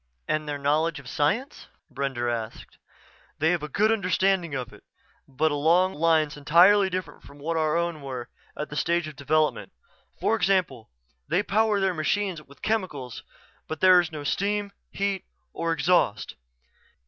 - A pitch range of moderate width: Yes, average, 4.3 semitones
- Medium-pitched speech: Yes, medium, 160 Hz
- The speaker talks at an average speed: Yes, average, 160 wpm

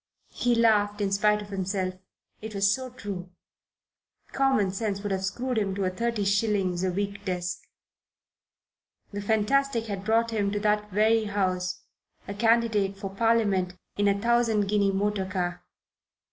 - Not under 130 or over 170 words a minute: Yes, average, 155 wpm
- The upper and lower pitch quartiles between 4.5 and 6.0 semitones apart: No, narrow, 2.4 semitones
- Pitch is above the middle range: Yes, high, 205 Hz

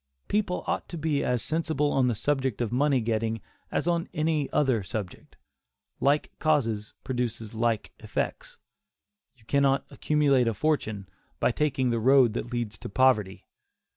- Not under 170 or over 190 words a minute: No, average, 150 wpm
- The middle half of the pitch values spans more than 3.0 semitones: Yes, average, 4.7 semitones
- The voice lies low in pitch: Yes, low, 130 Hz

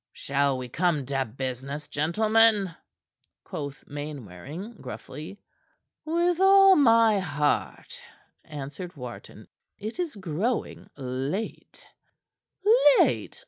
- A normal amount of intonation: No, wide, 8.2 semitones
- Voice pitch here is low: No, medium, 155 Hz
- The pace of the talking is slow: Yes, slow, 90 wpm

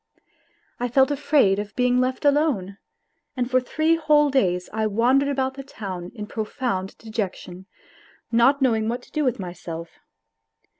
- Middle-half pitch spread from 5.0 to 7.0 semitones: Yes, wide, 5.5 semitones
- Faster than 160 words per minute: No, average, 155 wpm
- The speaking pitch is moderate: No, high, 245 Hz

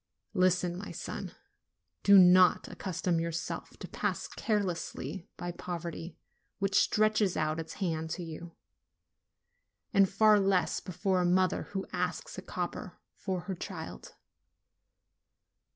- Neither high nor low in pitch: Yes, medium, 180 Hz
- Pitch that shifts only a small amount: Yes, narrow, 2.3 semitones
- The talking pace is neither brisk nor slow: No, slow, 120 wpm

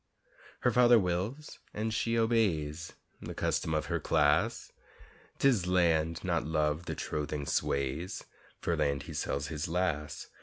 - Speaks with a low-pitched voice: Yes, very low, 85 Hz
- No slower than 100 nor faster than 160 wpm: Yes, average, 140 wpm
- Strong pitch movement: Yes, wide, 6.0 semitones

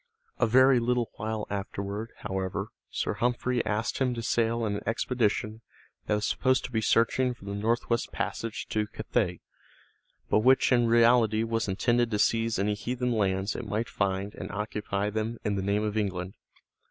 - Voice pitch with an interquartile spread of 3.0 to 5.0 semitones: No, narrow, 2.4 semitones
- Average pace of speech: Yes, average, 175 wpm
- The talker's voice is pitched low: Yes, low, 110 Hz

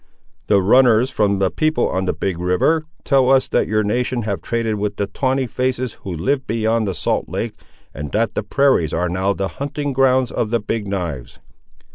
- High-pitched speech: No, low, 110 Hz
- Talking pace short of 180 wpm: No, average, 195 wpm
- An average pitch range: Yes, average, 4.9 semitones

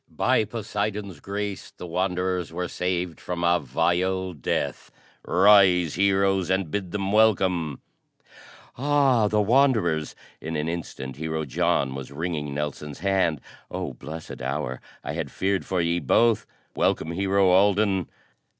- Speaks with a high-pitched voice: No, very low, 90 Hz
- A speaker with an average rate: No, slow, 130 wpm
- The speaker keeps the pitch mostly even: No, average, 3.7 semitones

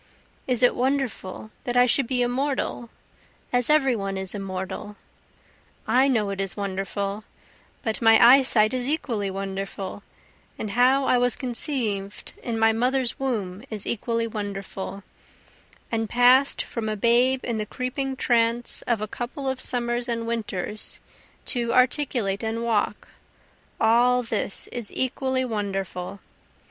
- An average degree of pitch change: Yes, average, 3.6 semitones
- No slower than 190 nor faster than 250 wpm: No, slow, 135 wpm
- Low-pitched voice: No, high, 230 Hz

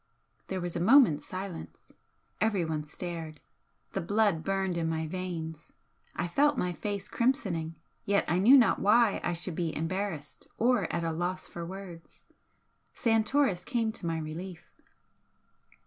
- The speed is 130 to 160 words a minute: Yes, average, 145 wpm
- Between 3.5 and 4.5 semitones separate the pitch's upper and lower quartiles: Yes, average, 4.1 semitones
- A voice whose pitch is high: No, medium, 180 Hz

